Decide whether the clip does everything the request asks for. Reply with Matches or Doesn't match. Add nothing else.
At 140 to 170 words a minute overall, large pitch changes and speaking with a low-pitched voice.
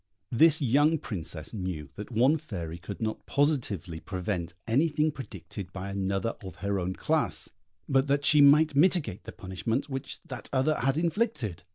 Matches